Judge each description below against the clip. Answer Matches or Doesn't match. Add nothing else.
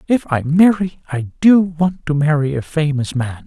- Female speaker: Doesn't match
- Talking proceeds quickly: Doesn't match